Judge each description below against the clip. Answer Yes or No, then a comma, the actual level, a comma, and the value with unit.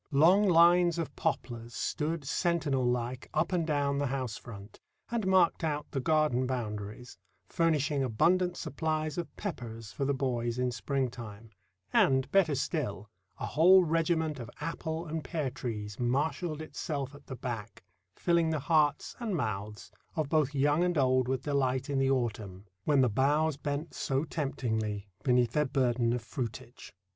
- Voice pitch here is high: No, medium, 140 Hz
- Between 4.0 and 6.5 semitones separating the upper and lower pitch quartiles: Yes, average, 4.5 semitones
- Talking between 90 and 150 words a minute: No, average, 160 wpm